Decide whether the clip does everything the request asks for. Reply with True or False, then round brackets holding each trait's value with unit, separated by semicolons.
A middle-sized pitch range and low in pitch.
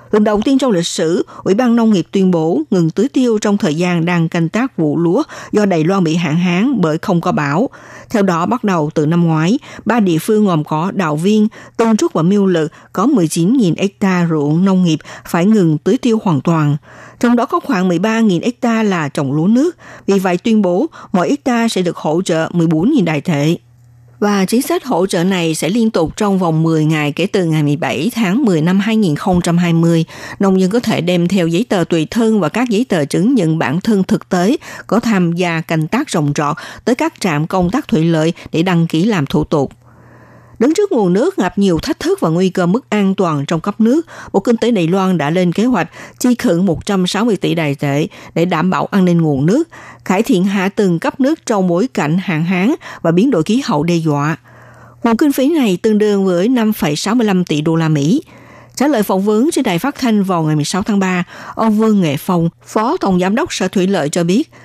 False (5.0 semitones; 185 Hz)